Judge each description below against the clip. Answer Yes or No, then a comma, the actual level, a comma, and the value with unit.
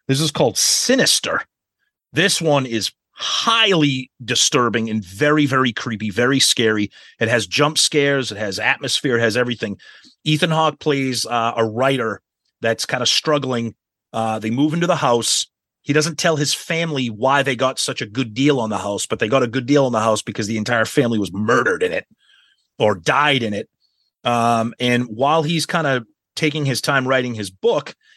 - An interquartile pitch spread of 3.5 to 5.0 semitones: Yes, average, 4.5 semitones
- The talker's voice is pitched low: Yes, low, 130 Hz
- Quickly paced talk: No, average, 190 wpm